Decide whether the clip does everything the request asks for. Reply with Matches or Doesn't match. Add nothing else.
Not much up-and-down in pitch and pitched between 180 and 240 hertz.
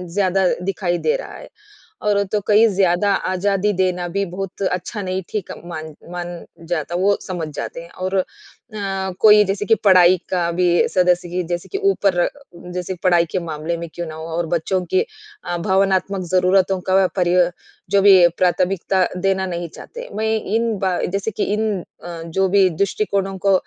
Matches